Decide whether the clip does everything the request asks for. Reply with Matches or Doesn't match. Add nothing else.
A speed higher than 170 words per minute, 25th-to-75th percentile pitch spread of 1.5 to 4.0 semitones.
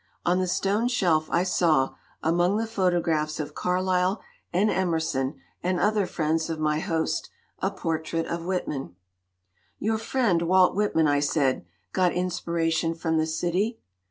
Doesn't match